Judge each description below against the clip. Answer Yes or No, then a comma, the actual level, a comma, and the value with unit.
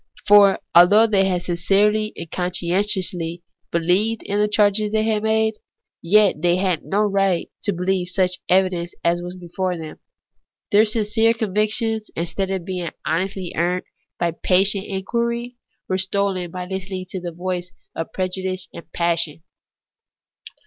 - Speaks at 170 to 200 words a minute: No, average, 150 wpm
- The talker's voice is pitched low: No, high, 190 Hz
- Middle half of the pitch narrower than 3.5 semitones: Yes, average, 2.9 semitones